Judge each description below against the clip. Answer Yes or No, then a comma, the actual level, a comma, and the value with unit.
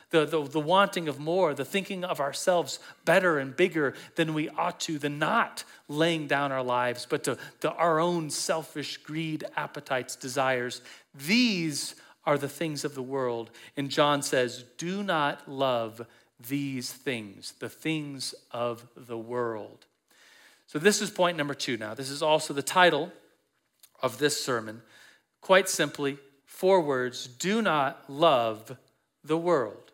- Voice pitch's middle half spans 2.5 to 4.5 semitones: Yes, average, 4.2 semitones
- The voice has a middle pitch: Yes, medium, 145 Hz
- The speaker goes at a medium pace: Yes, average, 150 wpm